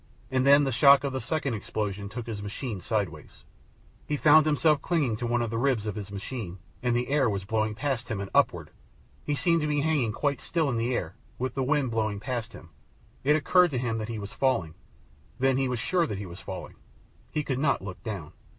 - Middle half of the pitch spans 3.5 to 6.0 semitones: Yes, average, 4.8 semitones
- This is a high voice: No, low, 120 Hz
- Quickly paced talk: Yes, fast, 230 wpm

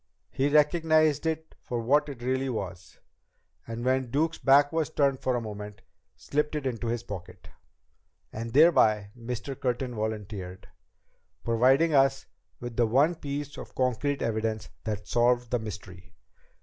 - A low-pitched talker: Yes, low, 125 Hz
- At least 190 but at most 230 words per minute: No, average, 145 wpm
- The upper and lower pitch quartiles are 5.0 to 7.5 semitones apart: No, average, 4.4 semitones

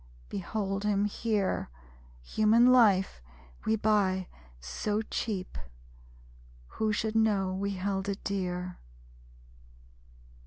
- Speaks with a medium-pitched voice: No, high, 200 Hz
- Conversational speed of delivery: No, slow, 90 wpm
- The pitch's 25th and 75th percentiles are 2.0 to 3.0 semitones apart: Yes, narrow, 2.4 semitones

